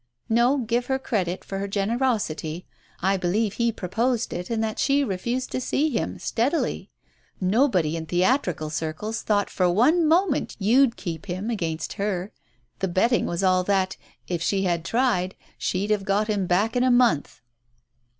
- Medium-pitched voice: No, high, 205 Hz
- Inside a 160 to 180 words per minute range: Yes, average, 170 wpm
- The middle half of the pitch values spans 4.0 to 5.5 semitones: Yes, average, 4.8 semitones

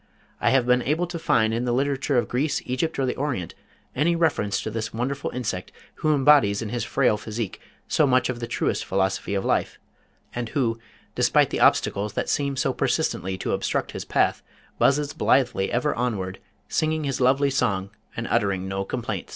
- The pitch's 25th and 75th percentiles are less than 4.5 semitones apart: No, average, 5.0 semitones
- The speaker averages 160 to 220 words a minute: Yes, average, 185 wpm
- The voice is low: Yes, low, 125 Hz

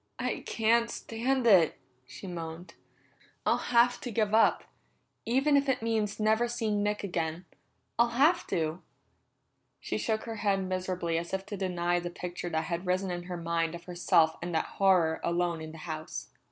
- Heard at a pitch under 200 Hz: Yes, medium, 185 Hz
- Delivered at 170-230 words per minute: Yes, average, 175 wpm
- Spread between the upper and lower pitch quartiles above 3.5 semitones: Yes, average, 4.7 semitones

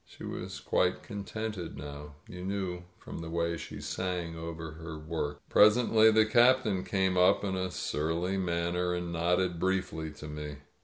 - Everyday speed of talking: Yes, average, 160 wpm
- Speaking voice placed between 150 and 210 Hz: No, very low, 90 Hz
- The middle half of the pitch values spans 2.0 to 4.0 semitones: Yes, average, 2.7 semitones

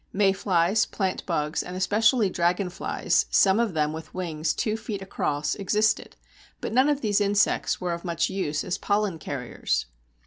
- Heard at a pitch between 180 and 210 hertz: Yes, high, 190 Hz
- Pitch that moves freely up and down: No, average, 3.7 semitones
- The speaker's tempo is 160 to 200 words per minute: No, average, 150 wpm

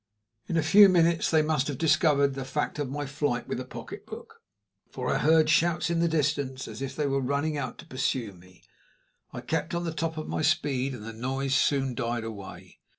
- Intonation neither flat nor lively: Yes, average, 3.5 semitones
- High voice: No, medium, 140 Hz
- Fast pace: Yes, fast, 215 wpm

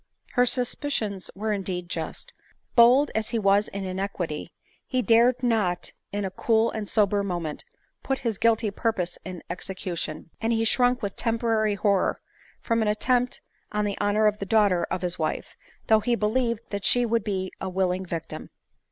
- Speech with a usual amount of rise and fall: Yes, average, 3.5 semitones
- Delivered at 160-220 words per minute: Yes, average, 170 wpm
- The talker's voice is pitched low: No, high, 210 Hz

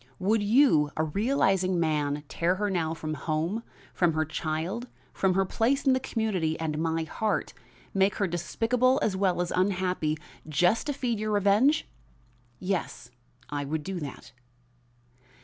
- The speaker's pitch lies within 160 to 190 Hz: Yes, medium, 185 Hz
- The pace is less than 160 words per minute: Yes, average, 150 wpm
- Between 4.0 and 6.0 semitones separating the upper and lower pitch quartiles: Yes, average, 5.3 semitones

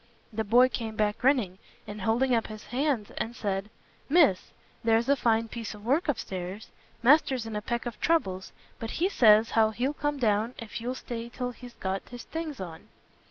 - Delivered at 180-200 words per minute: Yes, average, 190 wpm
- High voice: Yes, high, 230 Hz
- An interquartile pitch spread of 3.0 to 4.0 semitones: Yes, average, 3.3 semitones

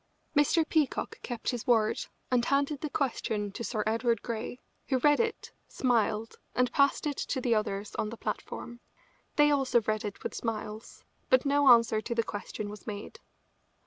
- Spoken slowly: No, average, 175 wpm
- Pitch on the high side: Yes, high, 235 Hz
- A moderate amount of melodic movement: Yes, average, 4.3 semitones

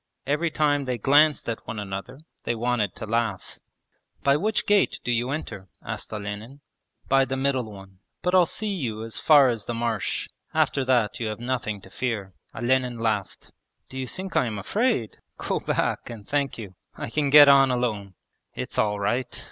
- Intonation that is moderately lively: Yes, average, 4.5 semitones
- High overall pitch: No, low, 120 Hz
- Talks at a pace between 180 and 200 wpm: Yes, average, 185 wpm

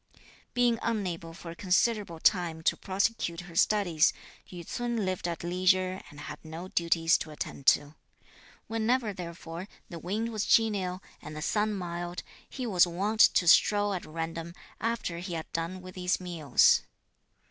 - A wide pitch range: No, average, 3.6 semitones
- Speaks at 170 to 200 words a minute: No, average, 160 wpm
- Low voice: No, medium, 180 Hz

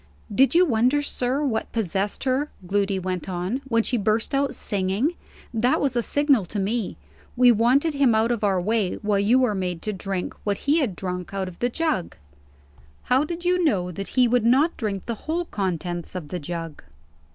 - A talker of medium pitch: No, high, 220 Hz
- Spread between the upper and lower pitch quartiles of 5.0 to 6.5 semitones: Yes, wide, 5.5 semitones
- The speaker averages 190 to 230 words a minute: Yes, average, 195 wpm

